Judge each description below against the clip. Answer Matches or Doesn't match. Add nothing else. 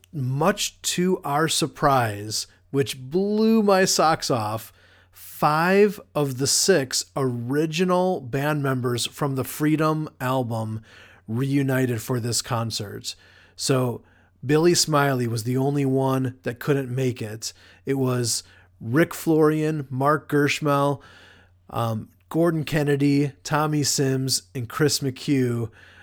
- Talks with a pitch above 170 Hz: Doesn't match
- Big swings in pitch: Doesn't match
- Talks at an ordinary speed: Doesn't match